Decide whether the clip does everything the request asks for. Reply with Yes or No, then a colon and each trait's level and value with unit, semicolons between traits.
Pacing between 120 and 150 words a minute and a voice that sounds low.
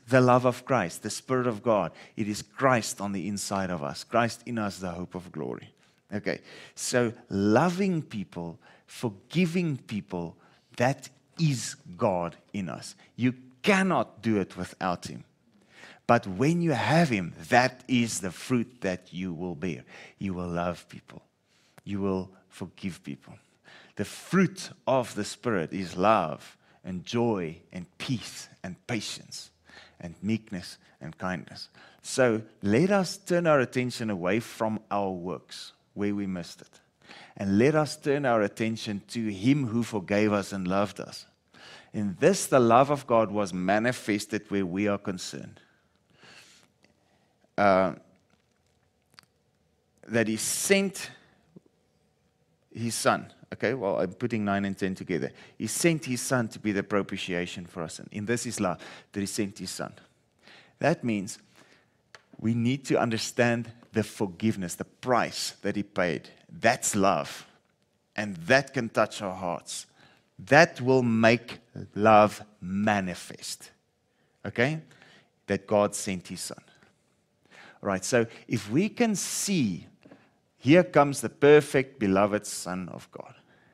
Yes: average, 145 wpm; low, 110 Hz